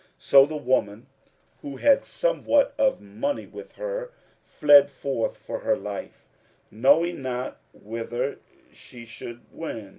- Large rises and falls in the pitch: Yes, wide, 6.2 semitones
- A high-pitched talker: No, low, 135 Hz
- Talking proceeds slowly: Yes, slow, 125 wpm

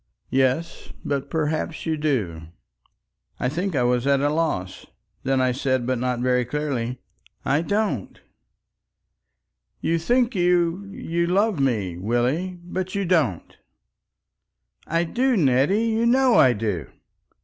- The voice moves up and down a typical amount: No, wide, 6.1 semitones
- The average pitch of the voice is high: No, medium, 150 Hz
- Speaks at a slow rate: Yes, slow, 125 wpm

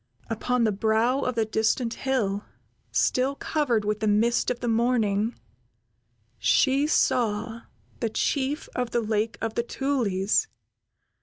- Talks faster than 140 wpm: No, slow, 135 wpm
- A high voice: Yes, high, 230 Hz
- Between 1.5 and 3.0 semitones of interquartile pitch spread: Yes, average, 2.7 semitones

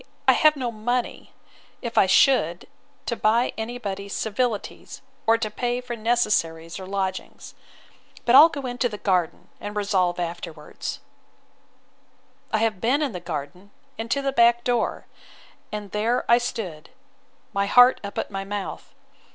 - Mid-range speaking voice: No, high, 215 Hz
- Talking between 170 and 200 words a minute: No, average, 150 wpm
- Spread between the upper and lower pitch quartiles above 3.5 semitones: Yes, average, 4.1 semitones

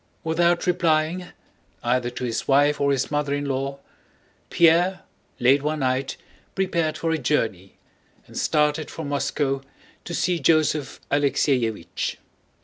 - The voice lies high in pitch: No, medium, 145 Hz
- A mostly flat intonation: No, average, 3.2 semitones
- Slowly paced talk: Yes, slow, 130 wpm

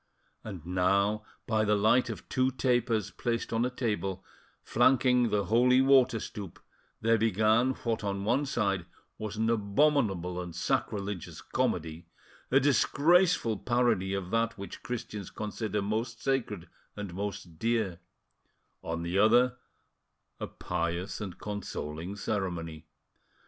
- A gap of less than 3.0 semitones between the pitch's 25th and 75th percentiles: No, average, 3.9 semitones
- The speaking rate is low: Yes, slow, 130 wpm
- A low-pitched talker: Yes, low, 105 Hz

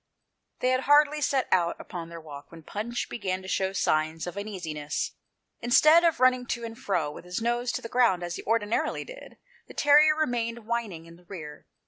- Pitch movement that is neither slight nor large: No, wide, 6.3 semitones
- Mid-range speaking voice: No, high, 215 Hz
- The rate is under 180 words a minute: No, average, 195 wpm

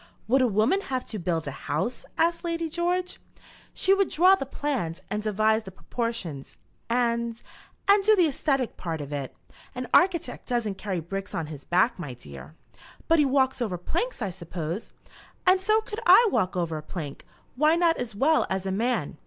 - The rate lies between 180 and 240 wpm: Yes, average, 185 wpm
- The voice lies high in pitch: Yes, high, 235 Hz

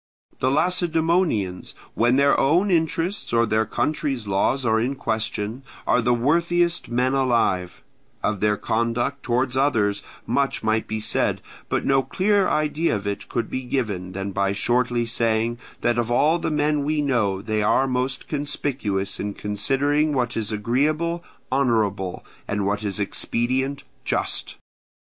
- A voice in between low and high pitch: No, low, 120 Hz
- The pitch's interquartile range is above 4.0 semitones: Yes, average, 5.1 semitones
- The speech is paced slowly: No, average, 150 wpm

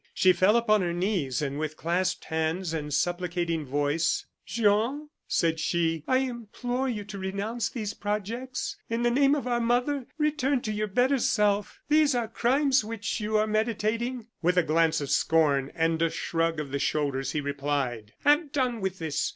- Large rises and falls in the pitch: Yes, wide, 6.8 semitones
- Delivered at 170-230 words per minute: Yes, average, 175 wpm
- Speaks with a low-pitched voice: No, high, 200 Hz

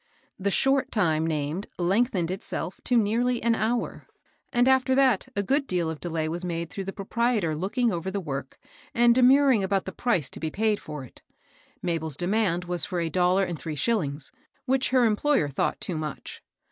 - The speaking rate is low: No, average, 185 wpm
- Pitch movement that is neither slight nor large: No, wide, 6.2 semitones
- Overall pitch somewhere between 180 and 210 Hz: Yes, high, 190 Hz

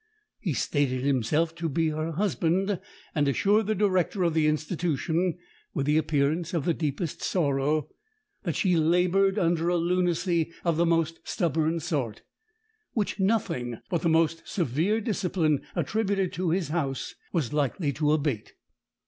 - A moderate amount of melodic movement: Yes, average, 3.2 semitones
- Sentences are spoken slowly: No, average, 150 wpm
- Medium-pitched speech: Yes, medium, 165 Hz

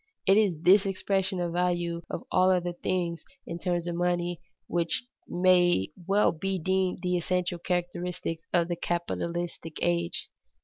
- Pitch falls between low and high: Yes, medium, 175 Hz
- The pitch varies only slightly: Yes, narrow, 1.3 semitones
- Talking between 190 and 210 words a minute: No, average, 150 wpm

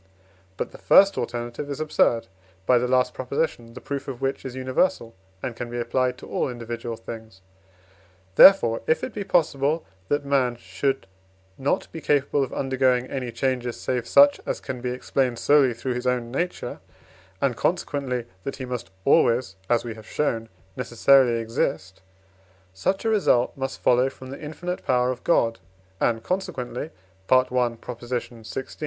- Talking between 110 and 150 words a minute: No, average, 160 wpm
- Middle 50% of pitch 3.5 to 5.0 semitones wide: No, narrow, 2.6 semitones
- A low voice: Yes, low, 125 Hz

